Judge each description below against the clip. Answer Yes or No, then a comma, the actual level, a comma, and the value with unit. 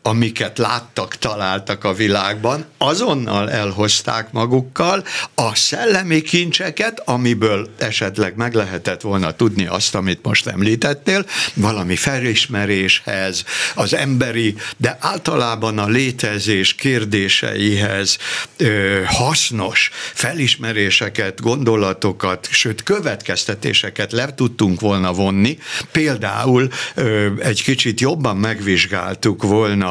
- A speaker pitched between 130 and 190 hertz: No, low, 110 Hz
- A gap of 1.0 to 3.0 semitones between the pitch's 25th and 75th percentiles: No, average, 3.8 semitones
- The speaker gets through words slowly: Yes, slow, 95 wpm